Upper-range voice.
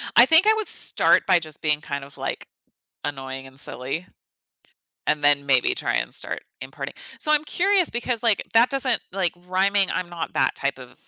No: medium, 175 Hz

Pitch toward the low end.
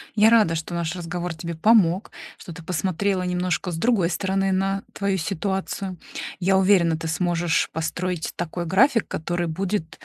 No: medium, 180 Hz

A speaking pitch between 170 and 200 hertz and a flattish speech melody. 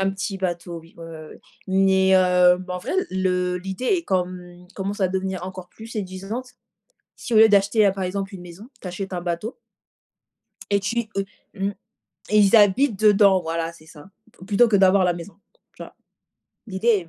Yes: high, 190 Hz; narrow, 2.0 semitones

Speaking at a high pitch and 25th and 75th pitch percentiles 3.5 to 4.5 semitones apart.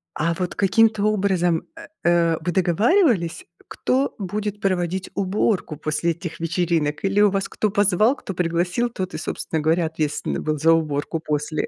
No: medium, 180 Hz; average, 3.8 semitones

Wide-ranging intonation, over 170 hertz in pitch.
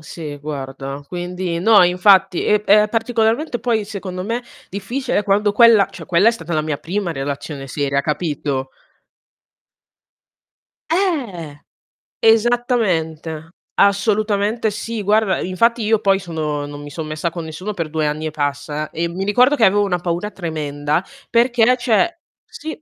Yes: wide, 6.0 semitones; medium, 185 Hz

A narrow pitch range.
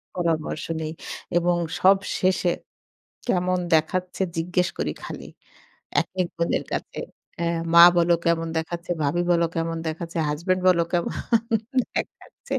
Yes: narrow, 1.7 semitones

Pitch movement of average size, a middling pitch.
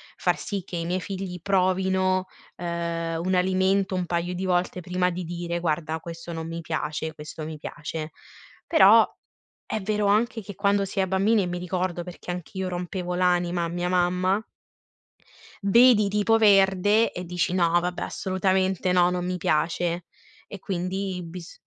No: narrow, 1.8 semitones; medium, 180 Hz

